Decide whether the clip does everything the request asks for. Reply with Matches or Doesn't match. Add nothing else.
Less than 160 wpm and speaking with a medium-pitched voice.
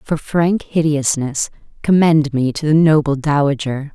Matches